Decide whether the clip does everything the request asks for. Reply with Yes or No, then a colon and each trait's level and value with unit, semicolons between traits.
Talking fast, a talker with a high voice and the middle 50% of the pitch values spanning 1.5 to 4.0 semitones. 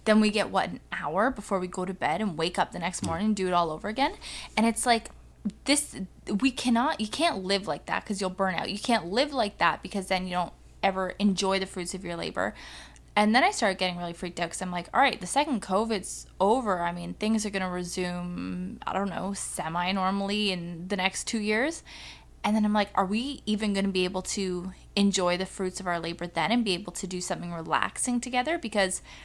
Yes: fast, 240 wpm; high, 195 Hz; average, 3.2 semitones